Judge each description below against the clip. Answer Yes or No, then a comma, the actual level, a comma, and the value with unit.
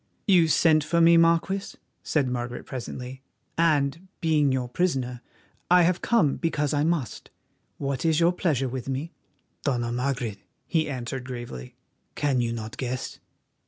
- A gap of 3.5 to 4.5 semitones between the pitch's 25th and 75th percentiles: No, average, 4.9 semitones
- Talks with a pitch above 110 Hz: Yes, medium, 140 Hz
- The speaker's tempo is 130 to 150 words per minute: Yes, average, 145 wpm